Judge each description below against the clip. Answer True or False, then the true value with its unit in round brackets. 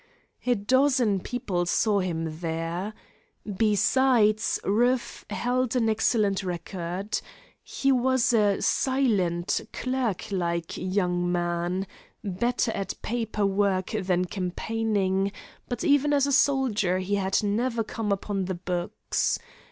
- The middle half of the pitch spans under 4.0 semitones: False (4.7 semitones)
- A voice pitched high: True (205 Hz)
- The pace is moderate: False (115 wpm)